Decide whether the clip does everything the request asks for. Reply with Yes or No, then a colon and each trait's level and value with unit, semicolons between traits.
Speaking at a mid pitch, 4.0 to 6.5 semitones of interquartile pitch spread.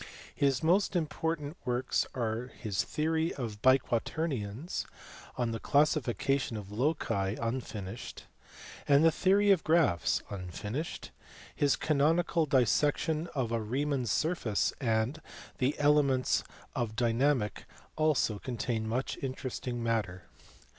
No: low, 130 Hz; average, 5.1 semitones